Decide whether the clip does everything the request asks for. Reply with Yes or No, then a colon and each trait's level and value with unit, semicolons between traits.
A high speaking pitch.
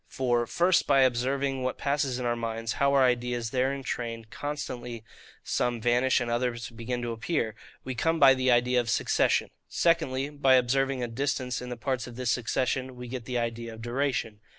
No: low, 125 Hz